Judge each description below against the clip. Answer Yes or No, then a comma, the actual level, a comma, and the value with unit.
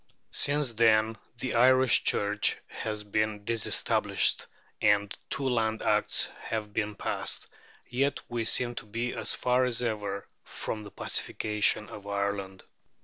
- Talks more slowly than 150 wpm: Yes, slow, 135 wpm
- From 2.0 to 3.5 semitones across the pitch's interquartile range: Yes, narrow, 2.6 semitones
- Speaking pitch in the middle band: No, low, 110 Hz